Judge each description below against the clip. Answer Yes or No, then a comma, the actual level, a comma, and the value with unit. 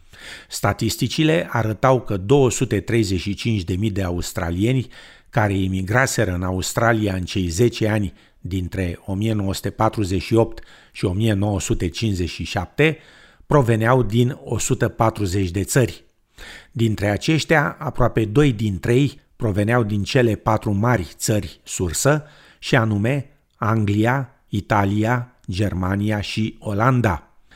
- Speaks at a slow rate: Yes, slow, 95 wpm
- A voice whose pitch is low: Yes, low, 110 Hz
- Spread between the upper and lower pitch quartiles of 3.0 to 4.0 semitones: Yes, average, 3.4 semitones